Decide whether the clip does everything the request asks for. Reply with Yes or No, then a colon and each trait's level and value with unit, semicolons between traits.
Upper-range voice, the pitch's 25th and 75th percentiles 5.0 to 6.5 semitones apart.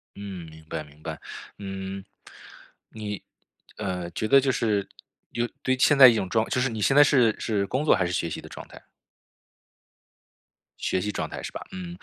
No: low, 105 Hz; average, 5.3 semitones